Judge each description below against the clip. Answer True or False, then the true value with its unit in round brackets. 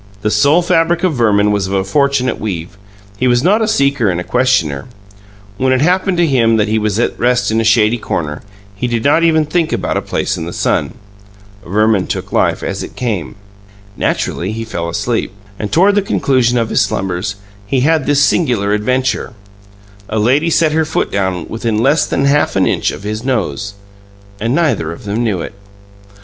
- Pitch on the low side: True (115 Hz)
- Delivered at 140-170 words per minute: False (195 wpm)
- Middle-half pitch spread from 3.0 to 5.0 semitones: False (5.6 semitones)